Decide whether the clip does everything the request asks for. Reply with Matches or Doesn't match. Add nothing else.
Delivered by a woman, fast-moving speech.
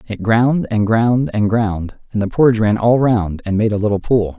Doesn't match